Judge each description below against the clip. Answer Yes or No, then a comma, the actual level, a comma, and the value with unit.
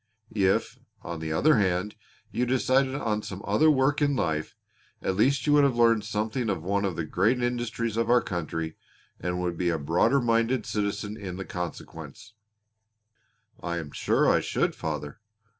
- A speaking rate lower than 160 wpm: No, average, 170 wpm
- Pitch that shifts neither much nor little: No, wide, 5.7 semitones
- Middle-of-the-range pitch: No, low, 105 Hz